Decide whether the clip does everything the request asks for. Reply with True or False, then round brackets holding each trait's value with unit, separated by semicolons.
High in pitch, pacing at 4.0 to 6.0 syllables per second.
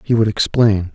False (105 Hz; 4.7 syllables/s)